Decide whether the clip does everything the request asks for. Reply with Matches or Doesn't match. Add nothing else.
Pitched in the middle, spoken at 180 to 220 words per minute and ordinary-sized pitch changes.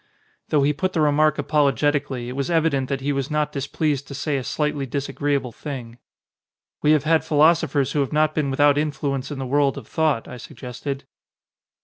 Doesn't match